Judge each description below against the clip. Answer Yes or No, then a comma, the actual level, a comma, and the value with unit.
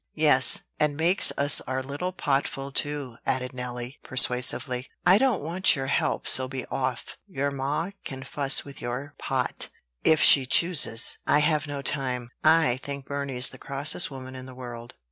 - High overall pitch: No, low, 135 Hz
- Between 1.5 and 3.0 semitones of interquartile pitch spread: Yes, narrow, 2.5 semitones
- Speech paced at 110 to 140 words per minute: No, average, 165 wpm